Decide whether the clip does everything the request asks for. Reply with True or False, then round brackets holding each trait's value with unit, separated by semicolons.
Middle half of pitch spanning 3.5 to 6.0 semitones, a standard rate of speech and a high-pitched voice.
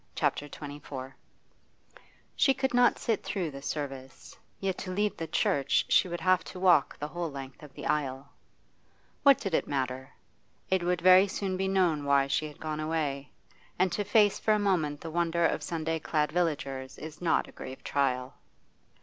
False (4.7 semitones; 180 wpm; 160 Hz)